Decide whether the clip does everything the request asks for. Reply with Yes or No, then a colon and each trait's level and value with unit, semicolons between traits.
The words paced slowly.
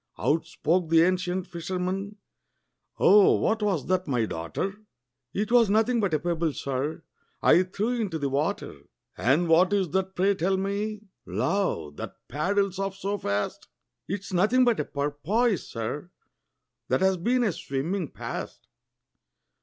No: average, 145 wpm